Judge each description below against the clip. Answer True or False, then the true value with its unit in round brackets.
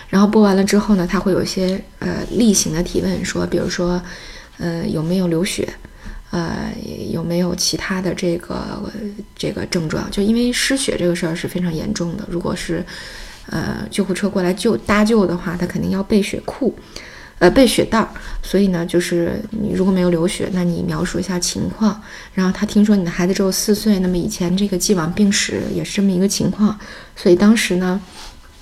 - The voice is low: False (185 Hz)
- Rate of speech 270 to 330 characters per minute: True (290 characters per minute)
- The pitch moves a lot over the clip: False (2.5 semitones)